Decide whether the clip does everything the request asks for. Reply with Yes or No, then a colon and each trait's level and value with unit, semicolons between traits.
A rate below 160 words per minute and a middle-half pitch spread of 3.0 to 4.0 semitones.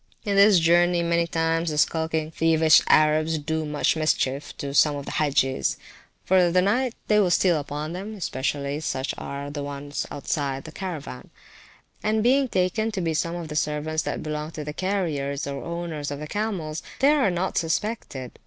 No: average, 195 wpm; average, 3.7 semitones